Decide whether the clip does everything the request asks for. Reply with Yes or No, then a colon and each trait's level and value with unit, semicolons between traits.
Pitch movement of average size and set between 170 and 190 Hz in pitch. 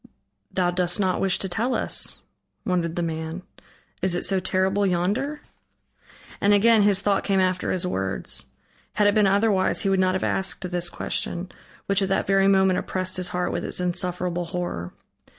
No: narrow, 1.8 semitones; medium, 185 Hz